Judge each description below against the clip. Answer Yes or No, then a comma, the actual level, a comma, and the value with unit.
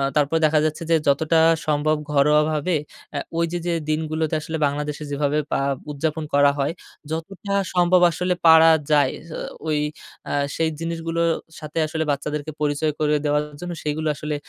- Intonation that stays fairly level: Yes, narrow, 1.7 semitones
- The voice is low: No, medium, 155 Hz